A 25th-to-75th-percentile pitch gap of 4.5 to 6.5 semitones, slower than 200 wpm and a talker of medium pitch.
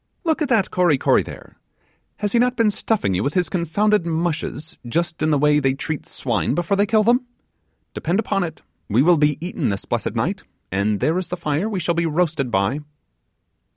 No: average, 5.3 semitones; fast, 205 wpm; medium, 170 Hz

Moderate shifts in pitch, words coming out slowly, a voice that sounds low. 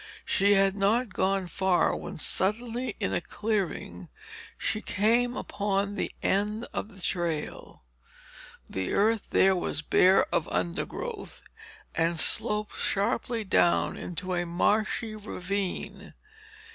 No: average, 3.1 semitones; slow, 120 wpm; high, 195 Hz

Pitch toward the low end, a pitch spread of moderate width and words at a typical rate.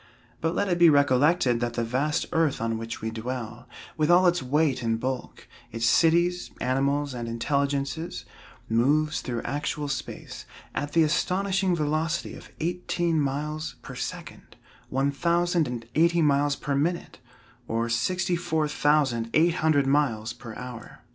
No: medium, 145 Hz; average, 4.8 semitones; average, 150 wpm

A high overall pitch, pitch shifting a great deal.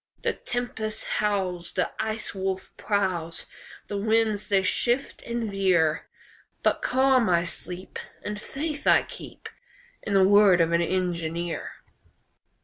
No: high, 195 Hz; average, 3.7 semitones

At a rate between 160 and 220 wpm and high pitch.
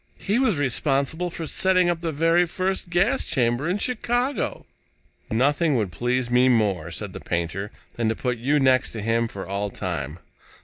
No: average, 175 wpm; low, 130 Hz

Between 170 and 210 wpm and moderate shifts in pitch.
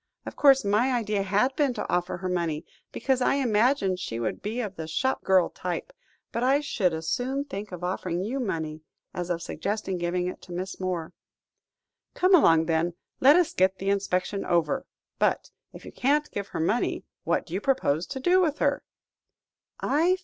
No: average, 185 wpm; wide, 6.8 semitones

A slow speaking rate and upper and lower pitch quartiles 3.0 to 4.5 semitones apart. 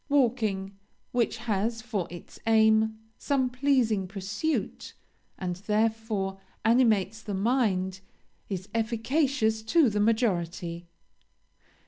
Yes: slow, 95 wpm; average, 3.5 semitones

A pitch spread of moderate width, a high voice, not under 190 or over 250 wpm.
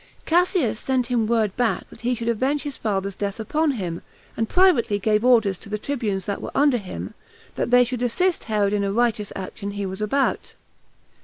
Yes: average, 4.0 semitones; high, 225 Hz; average, 200 wpm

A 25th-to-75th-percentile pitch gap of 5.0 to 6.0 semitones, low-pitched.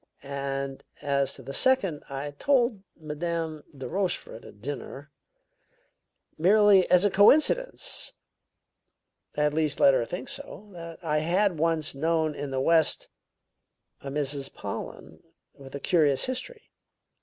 No: average, 5.3 semitones; medium, 155 Hz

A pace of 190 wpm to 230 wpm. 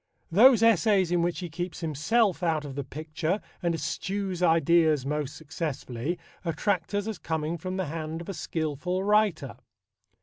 No: average, 160 wpm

